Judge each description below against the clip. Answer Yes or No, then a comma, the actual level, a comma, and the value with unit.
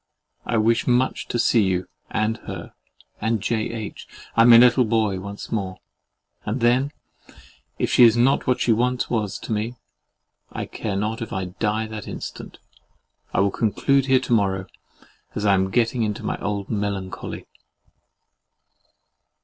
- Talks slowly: No, average, 160 wpm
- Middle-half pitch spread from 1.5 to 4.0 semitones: Yes, average, 2.9 semitones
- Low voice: Yes, low, 110 Hz